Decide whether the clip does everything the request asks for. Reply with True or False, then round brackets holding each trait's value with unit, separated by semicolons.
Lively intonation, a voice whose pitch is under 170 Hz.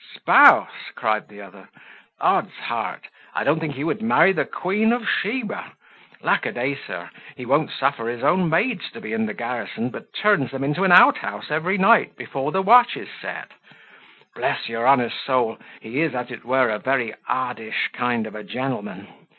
True (7.4 semitones; 135 Hz)